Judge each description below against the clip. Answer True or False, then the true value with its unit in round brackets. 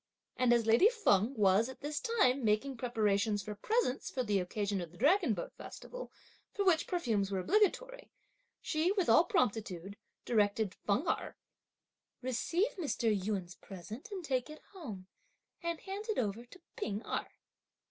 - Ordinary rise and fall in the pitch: False (8.8 semitones)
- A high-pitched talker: True (240 Hz)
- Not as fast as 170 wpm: True (160 wpm)